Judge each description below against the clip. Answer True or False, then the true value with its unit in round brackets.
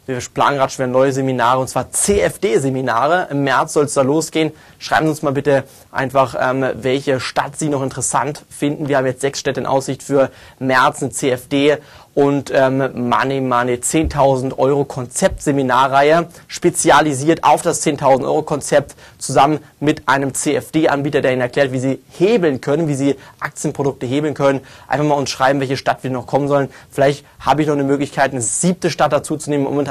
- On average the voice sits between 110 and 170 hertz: True (140 Hz)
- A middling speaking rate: True (180 wpm)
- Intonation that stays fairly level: True (2.1 semitones)